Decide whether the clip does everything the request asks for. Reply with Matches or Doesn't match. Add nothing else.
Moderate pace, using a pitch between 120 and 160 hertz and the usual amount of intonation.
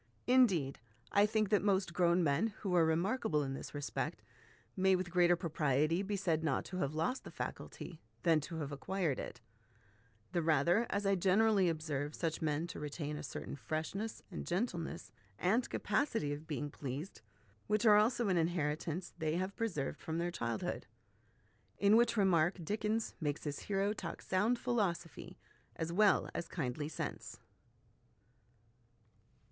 Doesn't match